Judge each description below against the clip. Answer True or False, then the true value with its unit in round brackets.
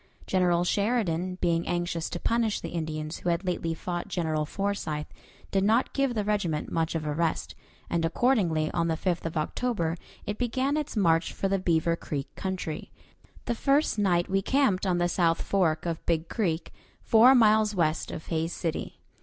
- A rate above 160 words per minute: True (180 wpm)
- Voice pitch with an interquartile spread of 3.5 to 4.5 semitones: True (4.1 semitones)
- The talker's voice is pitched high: False (175 Hz)